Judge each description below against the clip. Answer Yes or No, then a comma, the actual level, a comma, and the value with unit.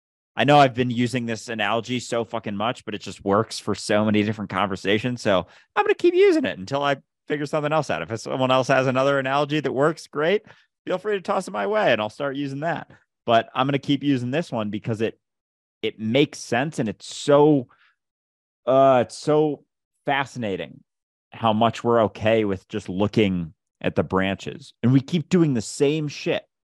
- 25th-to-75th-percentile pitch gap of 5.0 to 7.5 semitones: Yes, average, 5.3 semitones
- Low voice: Yes, low, 125 Hz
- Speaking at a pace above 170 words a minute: Yes, average, 200 wpm